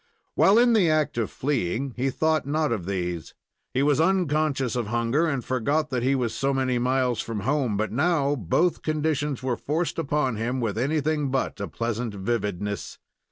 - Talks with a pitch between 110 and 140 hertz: Yes, low, 135 Hz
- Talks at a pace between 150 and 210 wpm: Yes, average, 180 wpm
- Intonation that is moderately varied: Yes, average, 4.5 semitones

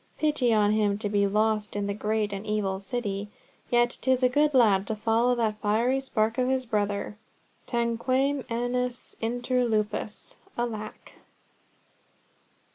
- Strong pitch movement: No, average, 2.9 semitones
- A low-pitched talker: No, high, 225 Hz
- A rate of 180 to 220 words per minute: No, slow, 135 wpm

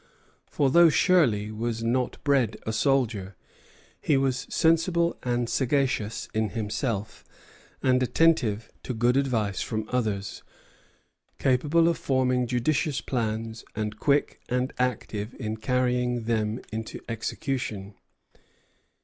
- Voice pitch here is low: Yes, low, 125 Hz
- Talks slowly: Yes, slow, 115 wpm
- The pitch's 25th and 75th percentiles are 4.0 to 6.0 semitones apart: No, average, 3.6 semitones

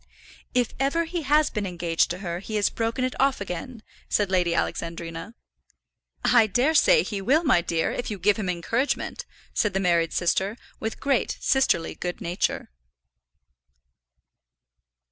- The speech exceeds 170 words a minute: No, average, 150 wpm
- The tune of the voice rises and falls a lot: Yes, wide, 6.6 semitones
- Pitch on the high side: Yes, high, 210 Hz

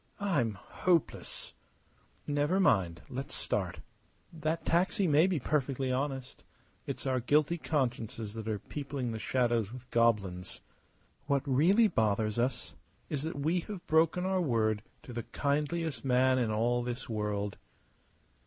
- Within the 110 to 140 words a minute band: Yes, slow, 135 wpm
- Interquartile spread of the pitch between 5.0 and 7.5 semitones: Yes, average, 5.3 semitones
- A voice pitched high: No, low, 130 Hz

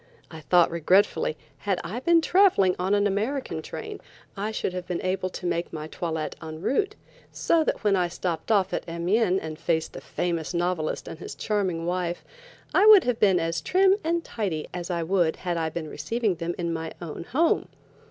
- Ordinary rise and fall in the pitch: Yes, average, 4.3 semitones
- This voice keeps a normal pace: Yes, average, 195 wpm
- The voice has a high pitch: No, medium, 180 Hz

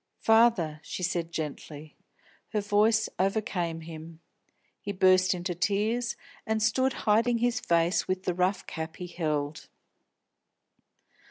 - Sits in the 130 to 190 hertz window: Yes, medium, 185 Hz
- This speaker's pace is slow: Yes, slow, 120 wpm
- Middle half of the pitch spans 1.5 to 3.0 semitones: No, average, 4.7 semitones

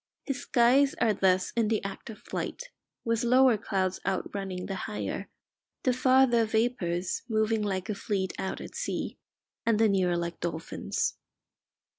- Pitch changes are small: No, average, 3.9 semitones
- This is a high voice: Yes, high, 215 Hz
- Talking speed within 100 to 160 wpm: Yes, average, 150 wpm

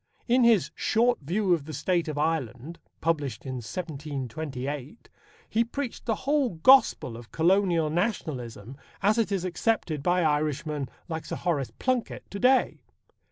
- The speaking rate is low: No, average, 145 wpm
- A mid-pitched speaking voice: Yes, medium, 165 Hz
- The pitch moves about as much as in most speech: No, wide, 6.6 semitones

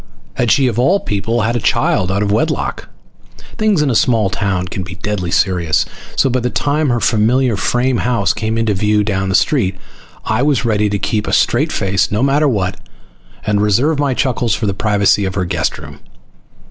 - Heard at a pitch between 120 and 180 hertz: No, low, 110 Hz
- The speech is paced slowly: No, average, 200 wpm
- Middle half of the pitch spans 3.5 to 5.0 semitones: Yes, average, 4.0 semitones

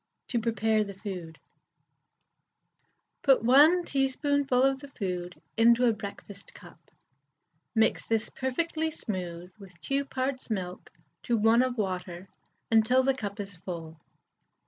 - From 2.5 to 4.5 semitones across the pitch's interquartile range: No, wide, 5.6 semitones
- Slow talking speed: Yes, slow, 125 wpm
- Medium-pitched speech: No, high, 225 Hz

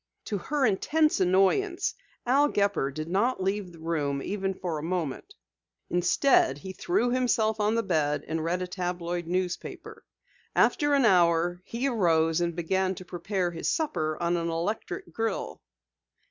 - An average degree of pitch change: Yes, average, 4.9 semitones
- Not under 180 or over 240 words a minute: No, average, 155 wpm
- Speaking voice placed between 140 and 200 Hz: Yes, medium, 185 Hz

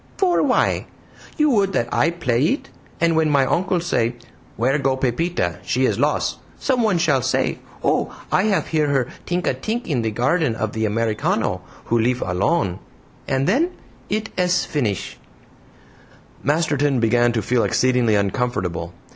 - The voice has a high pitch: No, low, 135 Hz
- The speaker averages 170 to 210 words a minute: No, average, 155 wpm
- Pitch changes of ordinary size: No, wide, 7.1 semitones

